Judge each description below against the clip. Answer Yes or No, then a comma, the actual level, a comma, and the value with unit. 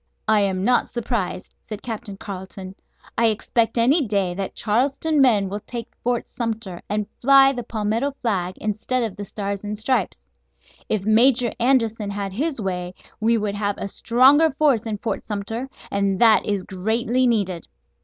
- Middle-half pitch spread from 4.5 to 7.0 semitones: No, average, 3.3 semitones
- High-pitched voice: Yes, high, 220 Hz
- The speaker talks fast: No, average, 165 wpm